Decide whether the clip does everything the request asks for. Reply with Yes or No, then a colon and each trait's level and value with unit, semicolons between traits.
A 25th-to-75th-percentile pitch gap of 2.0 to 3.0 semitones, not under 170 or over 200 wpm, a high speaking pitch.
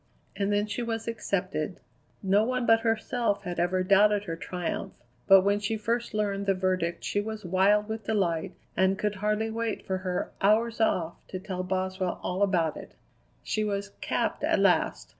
Yes: narrow, 2.5 semitones; average, 180 wpm; high, 200 Hz